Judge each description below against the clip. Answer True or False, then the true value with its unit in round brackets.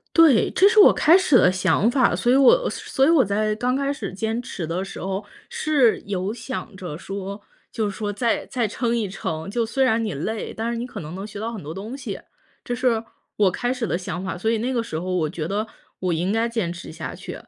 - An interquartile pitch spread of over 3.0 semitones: True (4.5 semitones)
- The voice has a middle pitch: False (220 Hz)